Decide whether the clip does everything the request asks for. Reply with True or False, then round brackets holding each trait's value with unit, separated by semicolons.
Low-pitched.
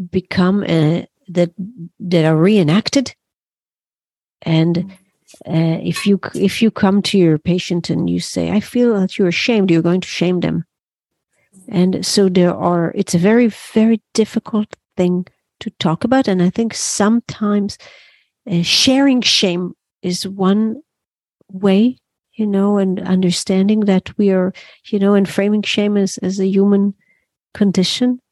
False (195 Hz)